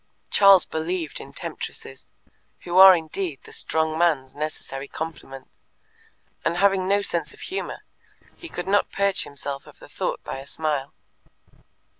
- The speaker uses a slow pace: No, average, 145 wpm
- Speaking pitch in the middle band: Yes, medium, 165 Hz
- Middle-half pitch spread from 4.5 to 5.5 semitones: Yes, average, 4.8 semitones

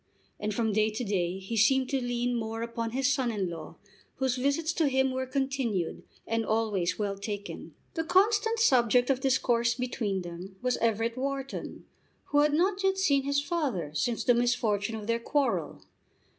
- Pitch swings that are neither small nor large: Yes, average, 4.1 semitones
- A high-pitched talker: Yes, high, 245 Hz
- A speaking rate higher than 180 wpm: No, average, 175 wpm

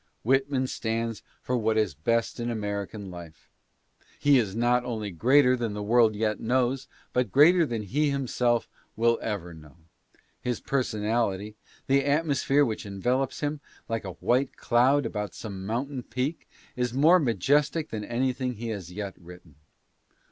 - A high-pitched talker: No, low, 120 Hz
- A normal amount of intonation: Yes, average, 4.1 semitones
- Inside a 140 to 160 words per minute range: Yes, average, 155 wpm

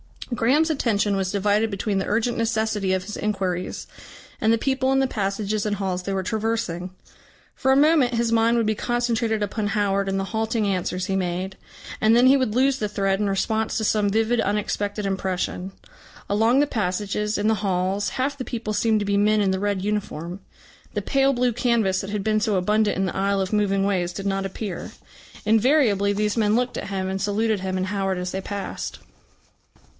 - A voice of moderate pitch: No, high, 210 Hz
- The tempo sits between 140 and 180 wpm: No, average, 200 wpm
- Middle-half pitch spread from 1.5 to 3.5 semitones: Yes, narrow, 2.6 semitones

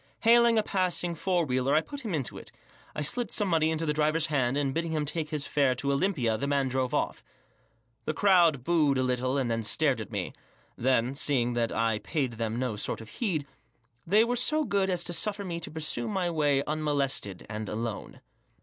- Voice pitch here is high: No, medium, 150 Hz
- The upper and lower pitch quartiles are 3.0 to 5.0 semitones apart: No, wide, 5.4 semitones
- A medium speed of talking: No, fast, 210 wpm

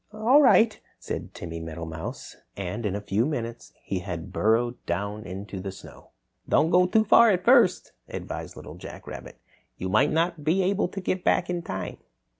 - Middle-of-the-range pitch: No, low, 120 Hz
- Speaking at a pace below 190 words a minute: Yes, average, 180 wpm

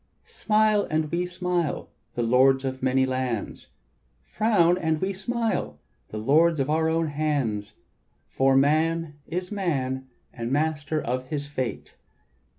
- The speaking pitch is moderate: Yes, medium, 150 Hz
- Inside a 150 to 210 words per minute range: No, slow, 135 wpm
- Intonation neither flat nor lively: Yes, average, 4.5 semitones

